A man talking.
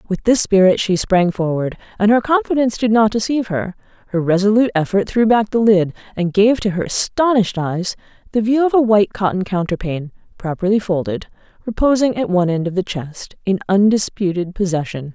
No: female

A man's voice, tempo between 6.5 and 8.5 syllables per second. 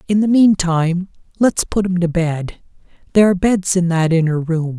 No: male; 5.3 syllables/s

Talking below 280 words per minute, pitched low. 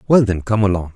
Yes: fast, 250 wpm; low, 100 Hz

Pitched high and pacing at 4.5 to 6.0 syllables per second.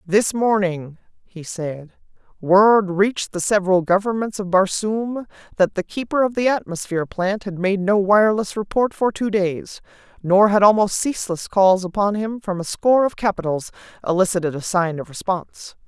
Yes: high, 195 Hz; 5.0 syllables/s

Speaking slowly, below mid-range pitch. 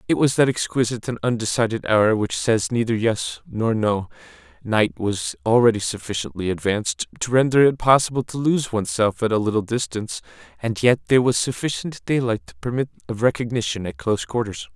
No: average, 170 wpm; low, 115 Hz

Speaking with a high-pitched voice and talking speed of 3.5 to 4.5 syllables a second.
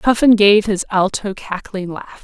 Yes: high, 200 Hz; 4.1 syllables/s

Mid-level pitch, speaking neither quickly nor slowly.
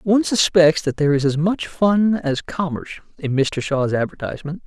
Yes: medium, 165 Hz; average, 180 wpm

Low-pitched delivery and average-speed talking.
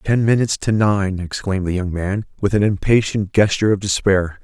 Yes: low, 100 Hz; average, 190 wpm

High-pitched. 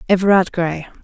No: medium, 180 Hz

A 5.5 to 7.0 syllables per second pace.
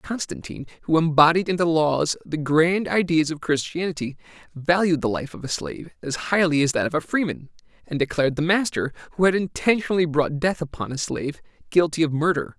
Yes: 5.8 syllables/s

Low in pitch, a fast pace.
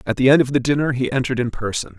Yes: low, 130 Hz; fast, 300 wpm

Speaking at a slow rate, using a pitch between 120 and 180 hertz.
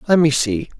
No: fast, 225 wpm; medium, 140 Hz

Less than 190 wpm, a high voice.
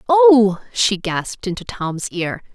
Yes: average, 140 wpm; high, 215 Hz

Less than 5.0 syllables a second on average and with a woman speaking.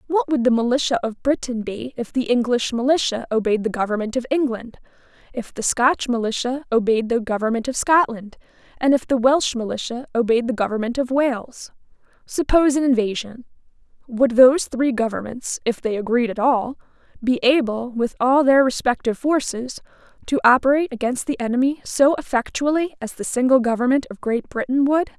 No: 5.3 syllables/s; female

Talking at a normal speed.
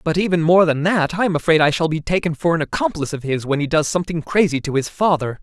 No: fast, 275 wpm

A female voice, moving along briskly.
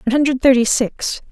No: female; average, 185 wpm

